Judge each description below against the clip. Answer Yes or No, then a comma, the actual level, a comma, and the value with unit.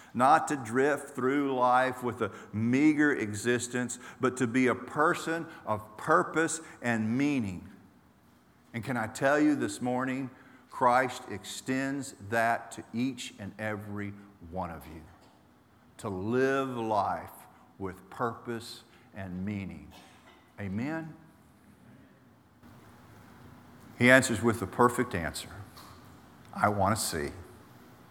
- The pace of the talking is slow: Yes, slow, 115 wpm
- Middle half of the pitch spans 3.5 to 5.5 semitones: Yes, average, 4.0 semitones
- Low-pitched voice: Yes, low, 120 Hz